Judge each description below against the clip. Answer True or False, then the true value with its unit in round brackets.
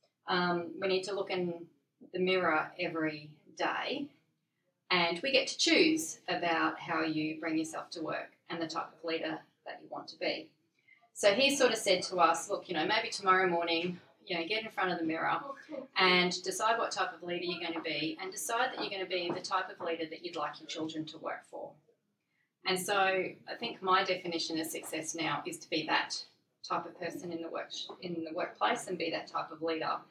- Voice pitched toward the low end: False (175 Hz)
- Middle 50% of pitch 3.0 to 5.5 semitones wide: False (2.5 semitones)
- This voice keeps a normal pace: False (220 wpm)